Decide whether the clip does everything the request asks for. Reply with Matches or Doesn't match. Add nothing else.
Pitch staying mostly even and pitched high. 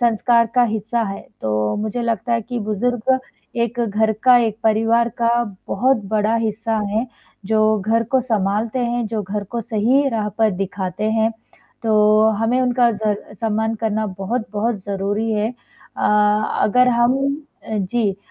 Matches